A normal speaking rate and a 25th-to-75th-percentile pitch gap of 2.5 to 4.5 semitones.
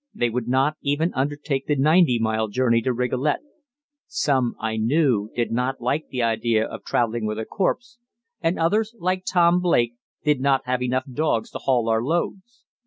No: average, 175 wpm; average, 5.0 semitones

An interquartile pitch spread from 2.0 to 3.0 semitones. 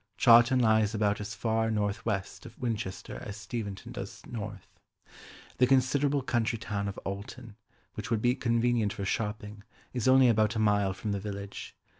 Yes: average, 2.7 semitones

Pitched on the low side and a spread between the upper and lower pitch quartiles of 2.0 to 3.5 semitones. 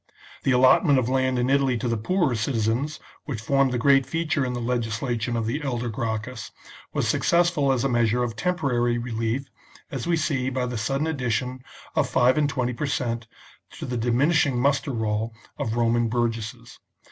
Yes: low, 125 Hz; average, 2.9 semitones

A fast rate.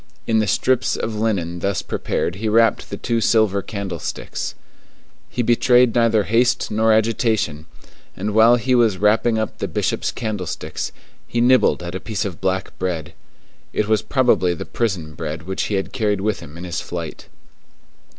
No: average, 170 wpm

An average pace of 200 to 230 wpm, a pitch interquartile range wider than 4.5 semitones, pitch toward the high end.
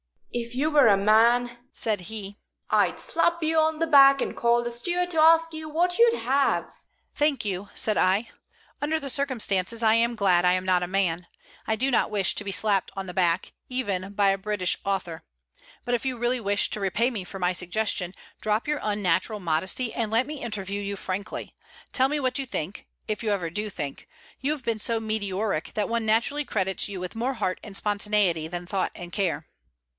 Yes: fast, 205 wpm; average, 5.0 semitones; high, 215 Hz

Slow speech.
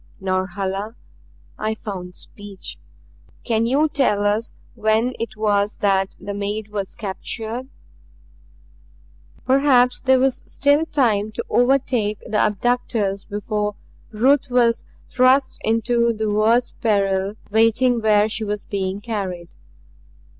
Yes: slow, 115 wpm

